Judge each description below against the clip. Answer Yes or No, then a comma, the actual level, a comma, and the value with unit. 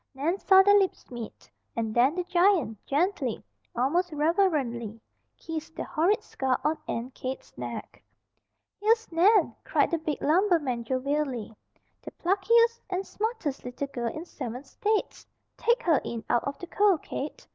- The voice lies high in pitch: Yes, very high, 315 Hz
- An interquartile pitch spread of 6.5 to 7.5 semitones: Yes, wide, 6.9 semitones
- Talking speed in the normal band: Yes, average, 150 wpm